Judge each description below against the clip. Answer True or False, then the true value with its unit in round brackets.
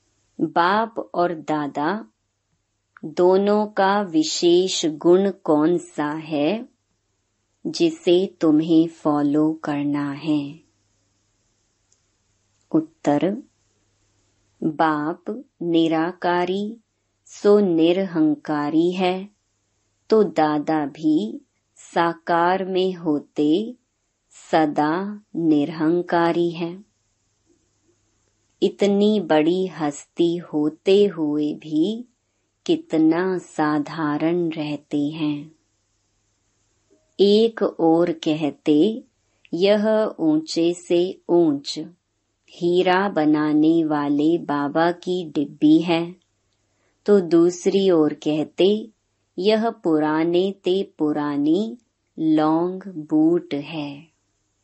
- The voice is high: False (160 Hz)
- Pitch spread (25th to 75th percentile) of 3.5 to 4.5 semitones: True (3.9 semitones)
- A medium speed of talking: False (70 wpm)